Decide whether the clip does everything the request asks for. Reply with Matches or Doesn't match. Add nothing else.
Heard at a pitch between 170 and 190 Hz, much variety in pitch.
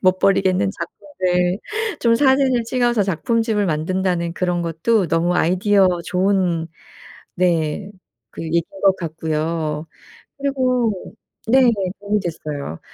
Doesn't match